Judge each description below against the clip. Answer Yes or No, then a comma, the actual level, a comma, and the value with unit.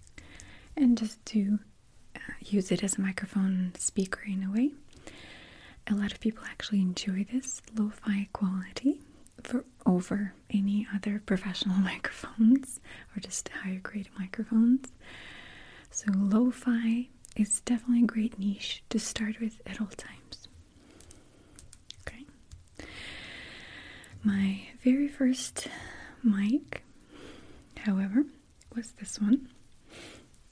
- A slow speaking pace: Yes, slow, 110 wpm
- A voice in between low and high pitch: No, high, 210 Hz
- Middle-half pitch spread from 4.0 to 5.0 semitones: No, average, 3.6 semitones